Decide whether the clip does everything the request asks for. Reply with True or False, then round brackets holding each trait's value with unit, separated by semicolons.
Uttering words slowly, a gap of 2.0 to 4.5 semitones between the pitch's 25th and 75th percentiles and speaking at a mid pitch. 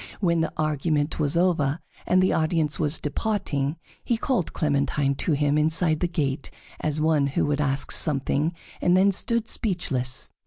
False (160 wpm; 3.4 semitones; 155 Hz)